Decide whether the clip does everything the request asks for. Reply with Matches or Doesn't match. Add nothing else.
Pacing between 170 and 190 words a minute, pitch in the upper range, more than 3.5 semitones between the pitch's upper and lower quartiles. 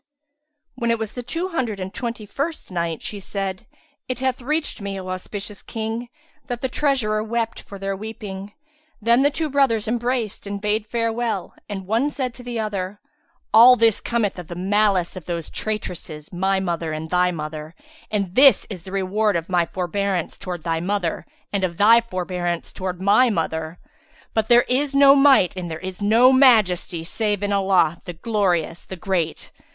Matches